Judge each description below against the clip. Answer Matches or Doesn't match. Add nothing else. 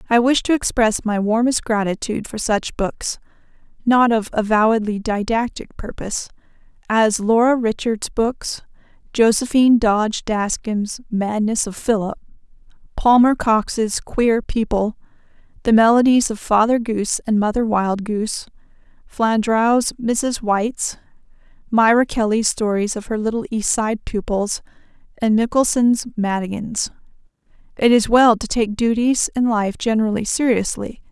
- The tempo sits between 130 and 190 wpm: Doesn't match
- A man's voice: Doesn't match